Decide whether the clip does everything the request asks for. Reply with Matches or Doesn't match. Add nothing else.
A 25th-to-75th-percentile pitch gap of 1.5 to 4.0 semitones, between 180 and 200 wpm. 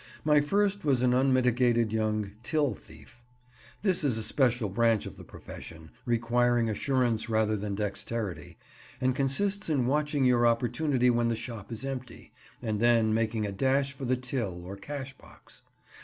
Doesn't match